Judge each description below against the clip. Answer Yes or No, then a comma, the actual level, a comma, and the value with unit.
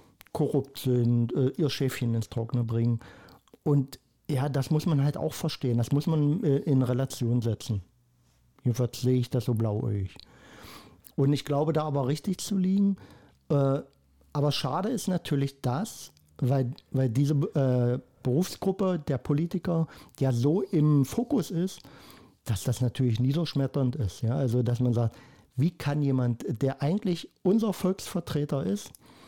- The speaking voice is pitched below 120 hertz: No, low, 135 Hz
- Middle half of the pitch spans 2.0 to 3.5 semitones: No, average, 4.0 semitones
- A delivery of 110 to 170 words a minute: Yes, average, 140 wpm